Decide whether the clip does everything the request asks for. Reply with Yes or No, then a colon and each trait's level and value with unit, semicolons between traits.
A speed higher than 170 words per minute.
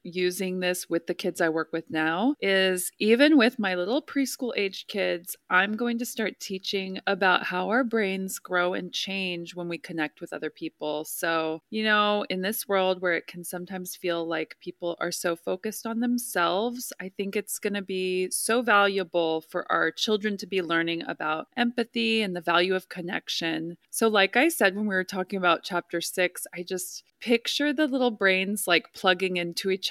Yes: average, 190 wpm